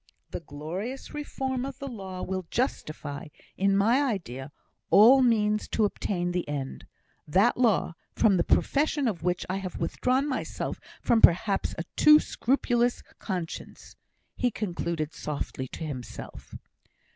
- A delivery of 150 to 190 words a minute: No, slow, 135 wpm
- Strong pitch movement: Yes, wide, 6.5 semitones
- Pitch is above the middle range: Yes, high, 200 Hz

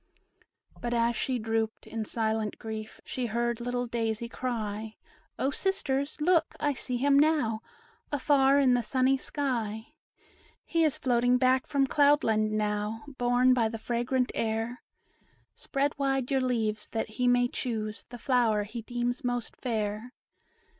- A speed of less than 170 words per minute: Yes, average, 145 wpm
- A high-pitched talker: Yes, high, 245 Hz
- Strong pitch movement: No, average, 3.0 semitones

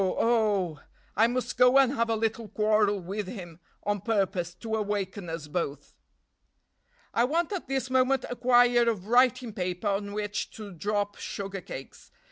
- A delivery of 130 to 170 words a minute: Yes, average, 160 wpm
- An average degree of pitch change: Yes, average, 3.8 semitones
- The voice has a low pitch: No, high, 210 Hz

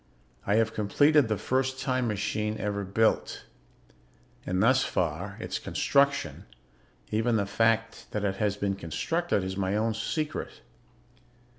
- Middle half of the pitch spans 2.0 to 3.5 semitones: No, average, 3.9 semitones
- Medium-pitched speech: No, low, 110 Hz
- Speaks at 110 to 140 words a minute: Yes, slow, 135 wpm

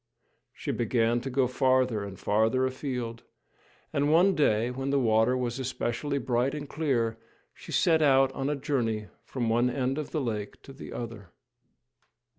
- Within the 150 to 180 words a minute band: Yes, average, 165 wpm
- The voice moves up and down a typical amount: Yes, average, 3.1 semitones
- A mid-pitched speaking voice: No, low, 125 Hz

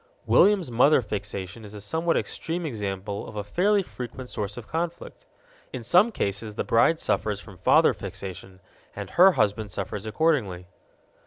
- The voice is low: Yes, low, 110 Hz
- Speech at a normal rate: Yes, average, 155 wpm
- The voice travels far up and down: Yes, wide, 8.1 semitones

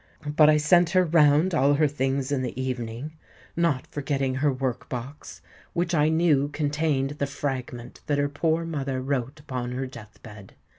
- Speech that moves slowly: No, average, 165 wpm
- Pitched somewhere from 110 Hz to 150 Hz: Yes, medium, 140 Hz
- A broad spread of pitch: No, average, 2.8 semitones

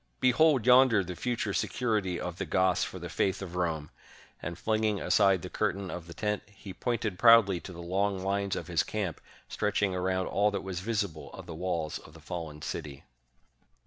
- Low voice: Yes, very low, 95 Hz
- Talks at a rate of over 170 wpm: Yes, average, 195 wpm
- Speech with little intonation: No, average, 3.1 semitones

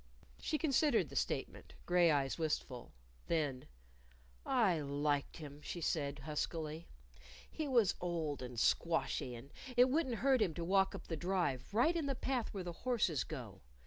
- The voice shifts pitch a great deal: Yes, wide, 8.1 semitones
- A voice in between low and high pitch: Yes, medium, 170 Hz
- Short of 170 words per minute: Yes, average, 160 wpm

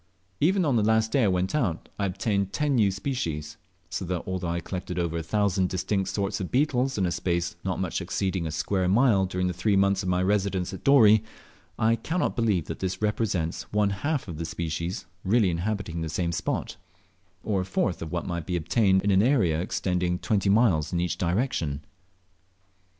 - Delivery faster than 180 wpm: Yes, average, 195 wpm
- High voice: No, very low, 95 Hz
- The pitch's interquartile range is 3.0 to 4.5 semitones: Yes, average, 3.5 semitones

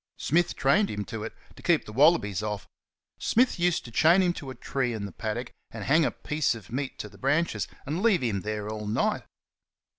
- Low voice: Yes, low, 130 Hz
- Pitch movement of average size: No, wide, 7.4 semitones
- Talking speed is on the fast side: Yes, fast, 215 wpm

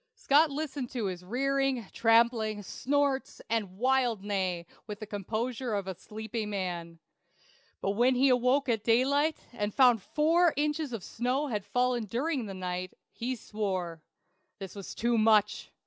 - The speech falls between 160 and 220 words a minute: No, average, 150 wpm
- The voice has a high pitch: Yes, high, 230 Hz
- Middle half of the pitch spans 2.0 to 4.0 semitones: No, average, 4.6 semitones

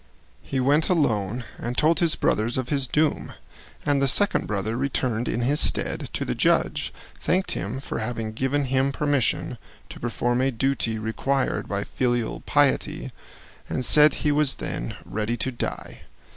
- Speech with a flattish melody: No, average, 3.7 semitones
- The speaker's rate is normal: Yes, average, 160 wpm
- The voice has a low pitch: Yes, low, 130 Hz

